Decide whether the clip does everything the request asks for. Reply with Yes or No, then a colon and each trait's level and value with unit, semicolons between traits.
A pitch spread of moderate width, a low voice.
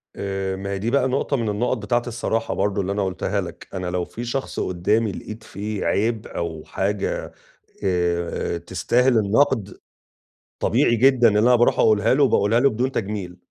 Yes: average, 3.8 semitones; low, 105 Hz